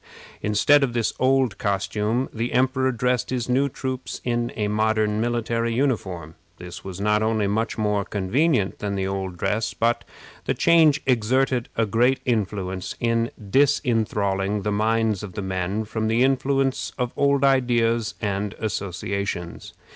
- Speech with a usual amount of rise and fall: Yes, average, 3.8 semitones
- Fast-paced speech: No, average, 145 wpm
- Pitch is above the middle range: No, low, 115 Hz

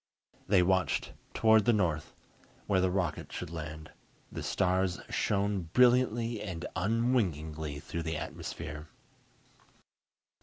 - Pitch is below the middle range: Yes, very low, 95 Hz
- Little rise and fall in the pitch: No, average, 4.8 semitones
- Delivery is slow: Yes, slow, 110 wpm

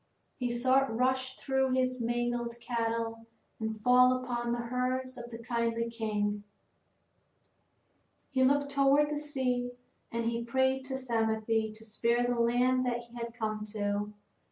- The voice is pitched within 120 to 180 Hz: No, high, 240 Hz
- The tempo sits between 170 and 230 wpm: No, average, 155 wpm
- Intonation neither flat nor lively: No, narrow, 2.0 semitones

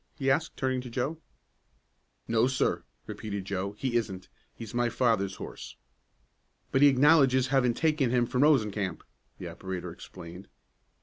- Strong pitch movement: No, average, 4.7 semitones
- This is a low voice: Yes, low, 120 Hz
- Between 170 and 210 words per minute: No, average, 140 wpm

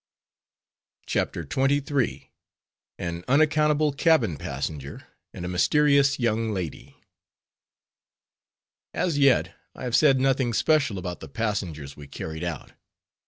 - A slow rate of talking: Yes, slow, 110 wpm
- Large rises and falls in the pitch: Yes, wide, 8.4 semitones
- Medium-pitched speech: No, low, 120 Hz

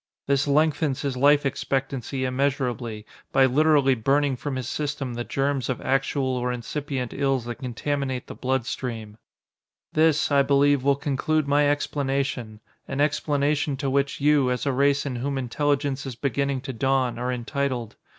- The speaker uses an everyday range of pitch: No, narrow, 2.0 semitones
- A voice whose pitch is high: No, low, 135 Hz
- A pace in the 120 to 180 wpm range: Yes, average, 160 wpm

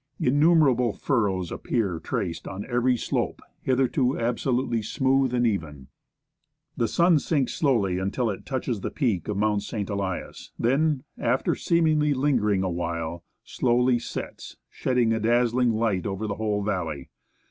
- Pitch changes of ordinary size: Yes, average, 4.7 semitones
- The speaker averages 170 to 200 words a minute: No, average, 140 wpm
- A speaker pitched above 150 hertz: No, low, 115 Hz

